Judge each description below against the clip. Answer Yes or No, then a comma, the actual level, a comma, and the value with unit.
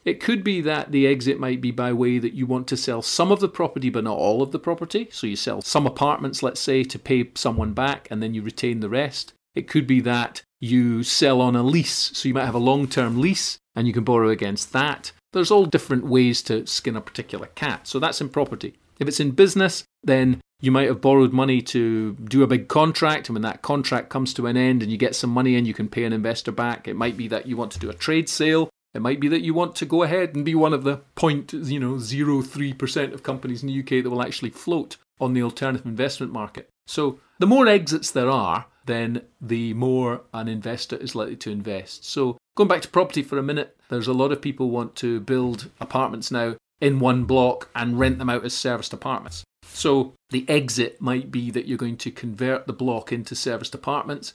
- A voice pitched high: No, low, 130 Hz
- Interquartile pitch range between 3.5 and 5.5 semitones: No, average, 2.9 semitones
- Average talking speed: No, fast, 235 wpm